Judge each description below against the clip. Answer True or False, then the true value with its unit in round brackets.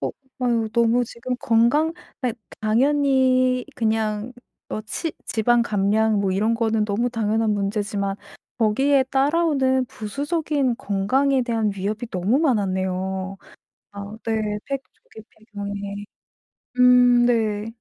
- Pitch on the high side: True (225 Hz)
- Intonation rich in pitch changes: False (3.5 semitones)